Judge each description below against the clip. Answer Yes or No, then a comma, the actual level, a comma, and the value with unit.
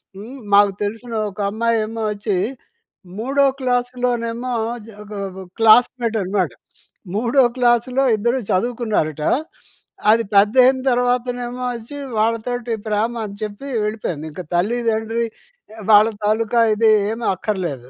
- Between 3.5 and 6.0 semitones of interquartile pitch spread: No, average, 2.8 semitones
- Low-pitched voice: No, high, 225 Hz